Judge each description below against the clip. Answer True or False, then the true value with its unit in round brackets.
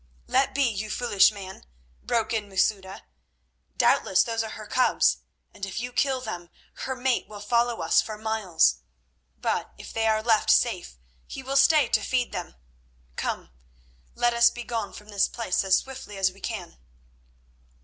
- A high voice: True (220 Hz)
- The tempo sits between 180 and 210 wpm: False (165 wpm)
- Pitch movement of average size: True (3.7 semitones)